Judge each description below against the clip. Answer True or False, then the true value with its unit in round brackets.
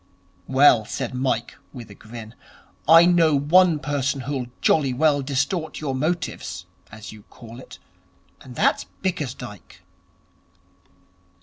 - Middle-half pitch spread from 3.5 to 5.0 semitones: True (4.3 semitones)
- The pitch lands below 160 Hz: True (135 Hz)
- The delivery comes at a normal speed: False (120 wpm)